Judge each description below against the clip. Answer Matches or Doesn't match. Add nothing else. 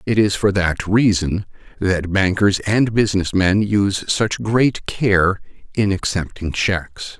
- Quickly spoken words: Doesn't match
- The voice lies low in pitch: Matches